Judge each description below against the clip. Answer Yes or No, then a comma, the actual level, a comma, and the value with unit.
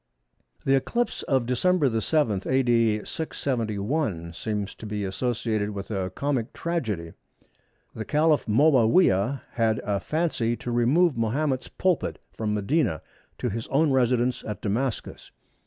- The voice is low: Yes, low, 120 Hz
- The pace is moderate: No, slow, 125 wpm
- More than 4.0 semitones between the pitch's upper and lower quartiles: Yes, average, 4.9 semitones